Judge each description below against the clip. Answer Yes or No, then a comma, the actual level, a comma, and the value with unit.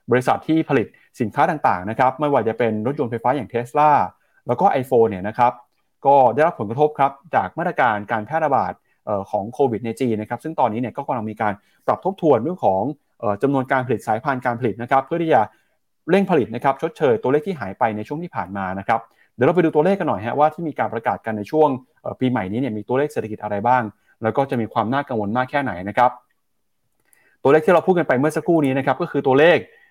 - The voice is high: No, low, 130 Hz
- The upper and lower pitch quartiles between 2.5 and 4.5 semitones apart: No, average, 5.1 semitones